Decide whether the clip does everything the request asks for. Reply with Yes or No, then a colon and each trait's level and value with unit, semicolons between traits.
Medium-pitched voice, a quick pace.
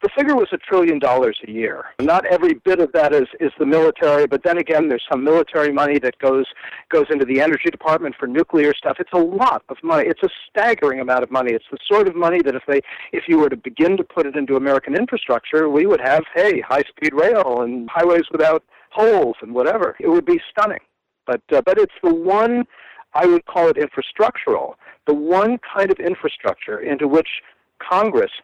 Yes: medium, 175 Hz; fast, 210 wpm